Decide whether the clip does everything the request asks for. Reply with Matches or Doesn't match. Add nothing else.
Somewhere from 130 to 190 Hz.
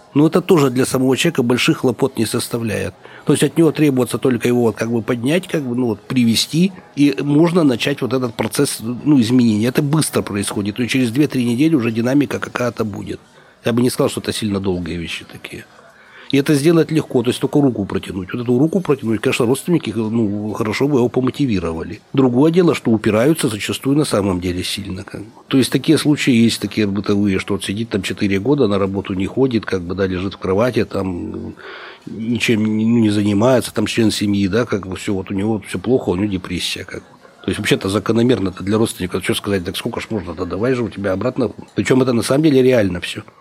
Doesn't match